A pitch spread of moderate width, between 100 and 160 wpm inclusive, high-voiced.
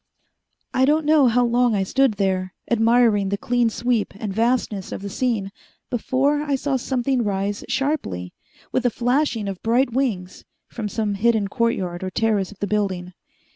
No: average, 4.1 semitones; average, 170 wpm; high, 230 Hz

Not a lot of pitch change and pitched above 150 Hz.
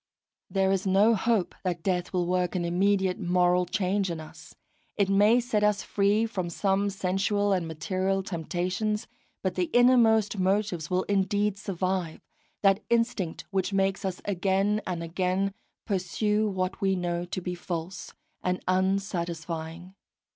Yes: narrow, 2.1 semitones; high, 190 Hz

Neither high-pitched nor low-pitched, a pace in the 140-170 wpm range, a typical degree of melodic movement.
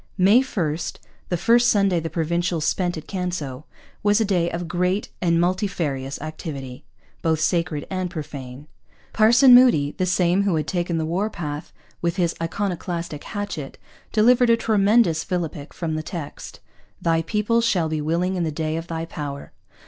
Yes: medium, 170 Hz; average, 165 wpm; average, 3.9 semitones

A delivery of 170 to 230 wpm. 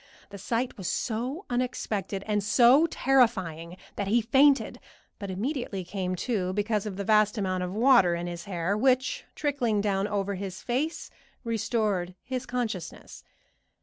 No: average, 150 wpm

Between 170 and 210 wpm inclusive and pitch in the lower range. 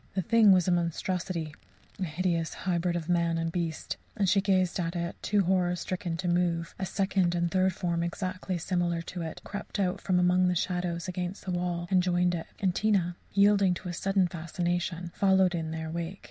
No: average, 200 wpm; medium, 180 Hz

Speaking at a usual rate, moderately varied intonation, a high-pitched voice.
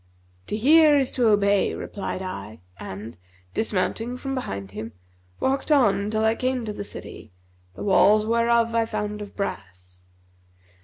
Yes: average, 150 wpm; average, 4.2 semitones; high, 210 Hz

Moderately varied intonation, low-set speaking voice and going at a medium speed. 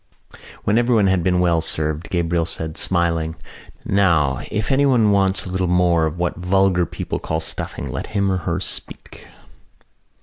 Yes: average, 3.0 semitones; very low, 90 Hz; average, 160 wpm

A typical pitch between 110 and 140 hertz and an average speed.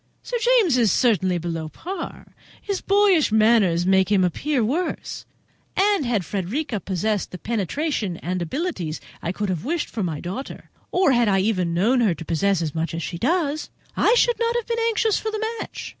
No: high, 220 Hz; average, 195 wpm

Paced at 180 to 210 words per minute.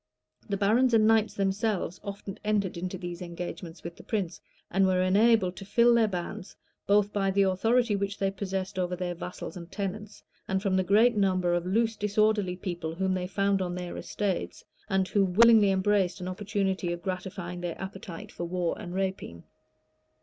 Yes: average, 185 wpm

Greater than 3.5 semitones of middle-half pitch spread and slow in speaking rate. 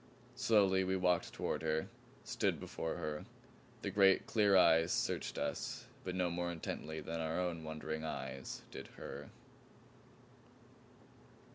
No: average, 3.0 semitones; slow, 130 wpm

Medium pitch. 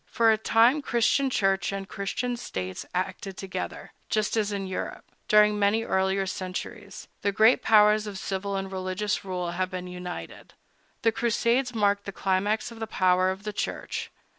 No: high, 200 Hz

